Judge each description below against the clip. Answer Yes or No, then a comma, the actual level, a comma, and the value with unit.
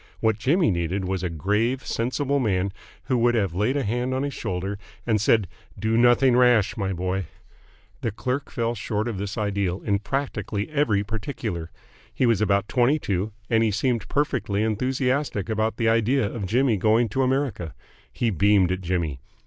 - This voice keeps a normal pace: Yes, average, 175 wpm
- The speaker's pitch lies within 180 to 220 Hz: No, low, 110 Hz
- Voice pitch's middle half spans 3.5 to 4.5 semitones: Yes, average, 4.0 semitones